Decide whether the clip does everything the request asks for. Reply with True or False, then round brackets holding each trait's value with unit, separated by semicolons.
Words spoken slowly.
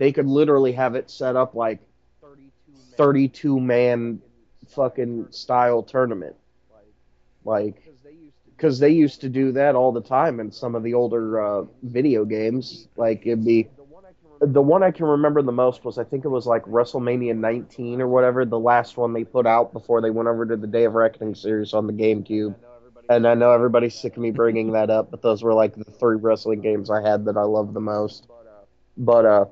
False (205 wpm)